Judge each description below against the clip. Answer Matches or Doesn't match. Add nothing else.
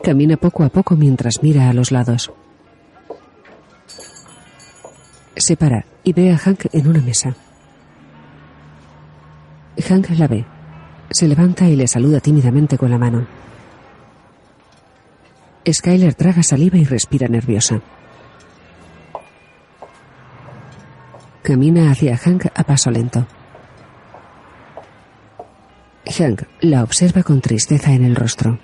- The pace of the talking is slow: Matches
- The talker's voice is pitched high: Doesn't match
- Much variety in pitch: Matches